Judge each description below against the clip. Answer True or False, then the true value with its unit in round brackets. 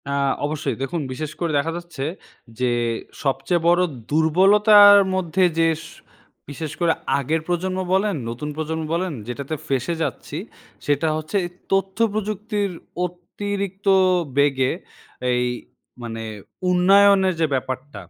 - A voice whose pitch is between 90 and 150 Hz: False (170 Hz)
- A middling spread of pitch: True (4.7 semitones)